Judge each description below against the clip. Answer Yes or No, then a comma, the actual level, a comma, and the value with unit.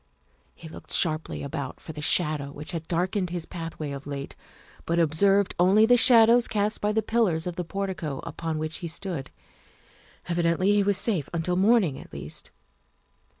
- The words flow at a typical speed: Yes, average, 170 wpm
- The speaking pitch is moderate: Yes, medium, 175 Hz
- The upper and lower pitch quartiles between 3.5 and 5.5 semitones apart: Yes, average, 4.3 semitones